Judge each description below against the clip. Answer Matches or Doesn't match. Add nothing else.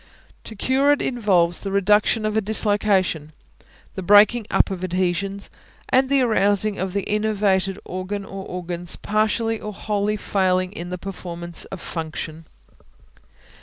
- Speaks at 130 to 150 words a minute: Matches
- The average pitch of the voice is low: Doesn't match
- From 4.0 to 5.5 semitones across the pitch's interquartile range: Doesn't match